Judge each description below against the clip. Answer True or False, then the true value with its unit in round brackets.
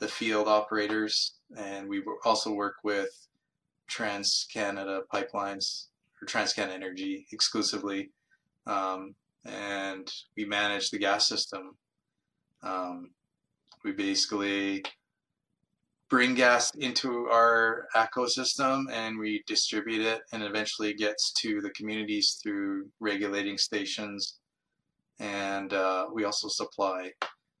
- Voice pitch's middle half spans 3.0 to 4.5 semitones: False (2.5 semitones)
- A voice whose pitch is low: True (105 Hz)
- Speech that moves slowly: True (105 wpm)